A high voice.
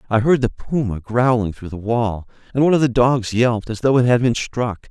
No: low, 120 Hz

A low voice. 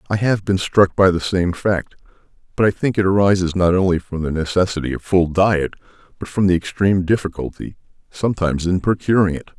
Yes: very low, 95 Hz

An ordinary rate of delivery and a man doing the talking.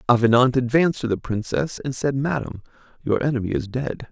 Yes: average, 175 wpm; male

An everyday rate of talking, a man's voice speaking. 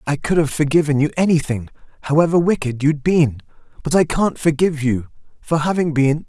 Yes: average, 160 wpm; male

